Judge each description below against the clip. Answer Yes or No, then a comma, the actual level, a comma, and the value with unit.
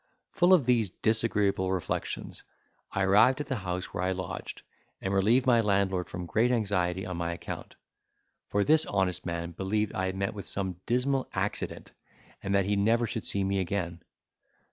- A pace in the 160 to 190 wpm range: Yes, average, 175 wpm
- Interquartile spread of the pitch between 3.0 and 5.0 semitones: Yes, average, 3.4 semitones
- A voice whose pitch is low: Yes, low, 100 Hz